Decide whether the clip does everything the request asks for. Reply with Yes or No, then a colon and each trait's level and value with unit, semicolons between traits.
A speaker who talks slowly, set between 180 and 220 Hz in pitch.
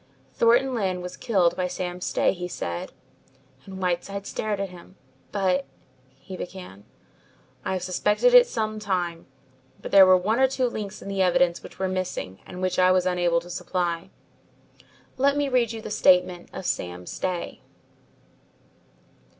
No: average, 165 wpm; medium, 185 Hz